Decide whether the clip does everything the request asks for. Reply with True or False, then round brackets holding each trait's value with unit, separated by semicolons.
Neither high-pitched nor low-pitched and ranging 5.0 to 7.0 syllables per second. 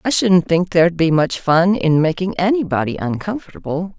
True (175 Hz; 5.2 syllables/s)